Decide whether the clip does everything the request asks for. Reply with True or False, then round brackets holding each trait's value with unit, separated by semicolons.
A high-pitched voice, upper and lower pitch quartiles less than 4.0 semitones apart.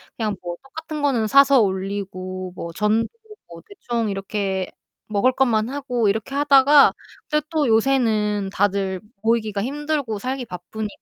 False (220 Hz; 5.4 semitones)